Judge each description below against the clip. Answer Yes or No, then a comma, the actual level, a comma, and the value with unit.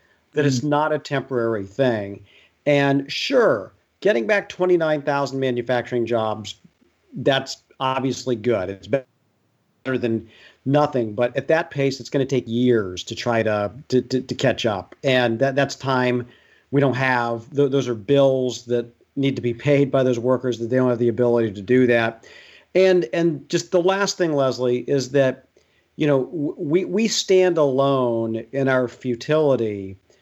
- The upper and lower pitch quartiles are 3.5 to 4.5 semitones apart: No, average, 2.8 semitones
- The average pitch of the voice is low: Yes, low, 130 Hz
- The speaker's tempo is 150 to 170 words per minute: Yes, average, 165 wpm